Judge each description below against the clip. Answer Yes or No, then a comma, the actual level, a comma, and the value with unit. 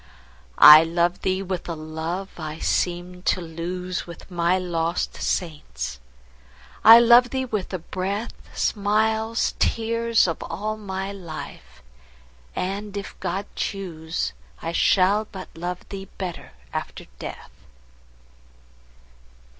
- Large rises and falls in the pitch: No, average, 3.7 semitones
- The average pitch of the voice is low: No, medium, 180 Hz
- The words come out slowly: Yes, slow, 110 wpm